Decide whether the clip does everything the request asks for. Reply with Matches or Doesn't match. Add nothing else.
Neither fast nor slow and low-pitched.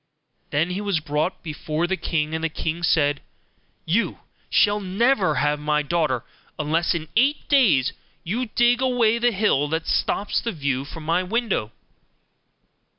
Doesn't match